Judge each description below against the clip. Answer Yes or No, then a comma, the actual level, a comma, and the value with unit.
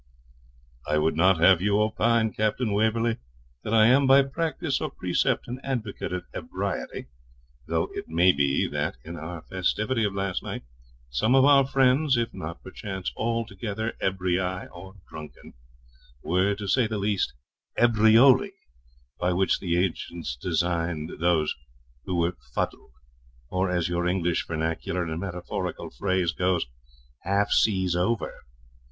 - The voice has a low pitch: Yes, very low, 95 Hz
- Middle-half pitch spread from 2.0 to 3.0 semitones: No, average, 4.3 semitones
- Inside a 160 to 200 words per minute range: No, average, 140 wpm